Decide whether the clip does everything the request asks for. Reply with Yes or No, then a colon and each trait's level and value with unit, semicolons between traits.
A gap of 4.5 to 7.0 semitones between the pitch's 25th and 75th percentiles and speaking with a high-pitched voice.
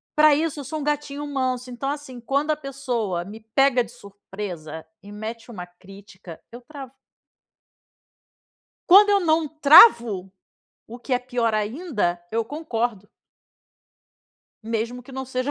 Yes: average, 5.3 semitones; high, 245 Hz